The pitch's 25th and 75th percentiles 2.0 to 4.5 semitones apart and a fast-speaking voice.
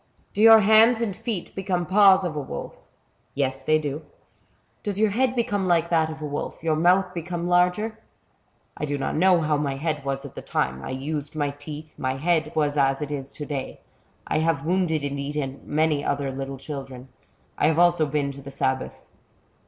Yes: average, 4.2 semitones; fast, 215 wpm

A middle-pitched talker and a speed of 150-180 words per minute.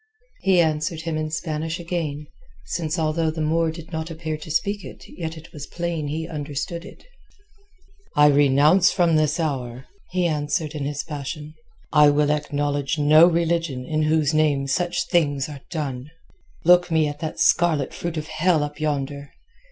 Yes: medium, 155 Hz; average, 165 wpm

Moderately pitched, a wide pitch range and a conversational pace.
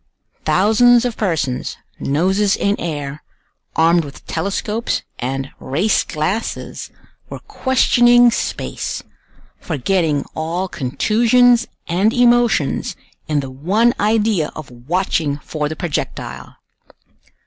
No: medium, 180 Hz; wide, 6.9 semitones; slow, 100 wpm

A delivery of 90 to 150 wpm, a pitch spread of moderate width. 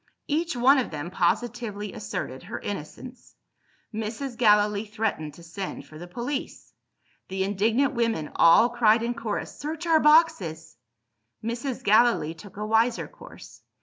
Yes: average, 140 wpm; average, 4.3 semitones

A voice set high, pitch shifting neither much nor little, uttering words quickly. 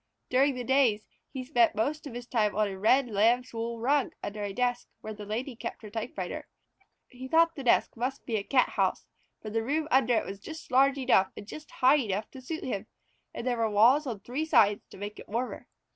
Yes: high, 245 Hz; average, 3.8 semitones; fast, 220 wpm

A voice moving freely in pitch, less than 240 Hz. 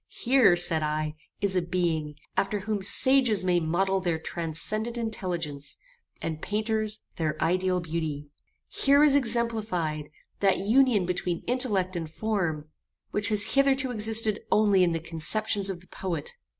No: average, 4.9 semitones; high, 190 Hz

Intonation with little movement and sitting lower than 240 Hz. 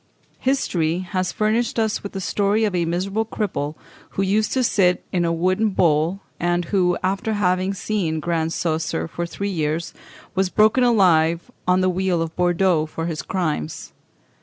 No: average, 3.2 semitones; medium, 185 Hz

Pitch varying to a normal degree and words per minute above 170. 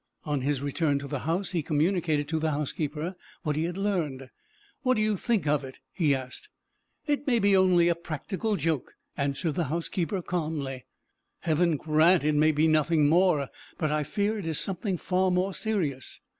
Yes: average, 4.0 semitones; average, 185 wpm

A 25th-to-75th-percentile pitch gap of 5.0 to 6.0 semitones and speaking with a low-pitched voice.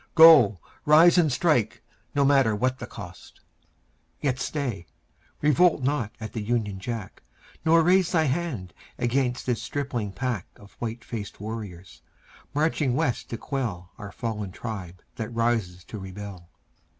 Yes: wide, 5.5 semitones; low, 120 Hz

